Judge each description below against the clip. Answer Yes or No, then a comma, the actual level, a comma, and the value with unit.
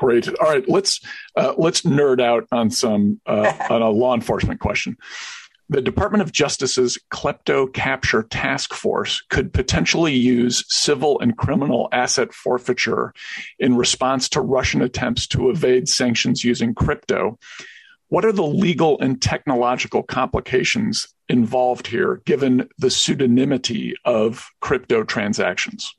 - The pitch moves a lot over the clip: Yes, wide, 7.6 semitones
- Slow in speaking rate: Yes, slow, 130 wpm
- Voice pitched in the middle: No, low, 130 Hz